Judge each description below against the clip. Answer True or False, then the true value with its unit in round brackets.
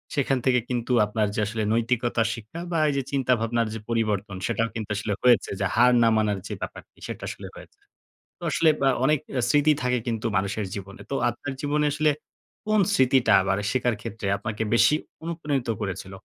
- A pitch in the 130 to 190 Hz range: False (115 Hz)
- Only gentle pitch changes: False (3.8 semitones)